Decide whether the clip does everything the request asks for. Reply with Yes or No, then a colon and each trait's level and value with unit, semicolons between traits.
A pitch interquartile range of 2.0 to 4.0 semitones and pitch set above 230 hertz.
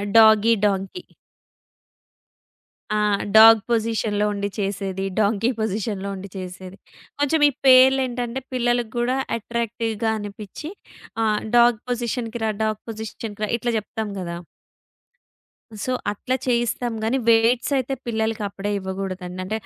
No: average, 2.9 semitones; high, 220 Hz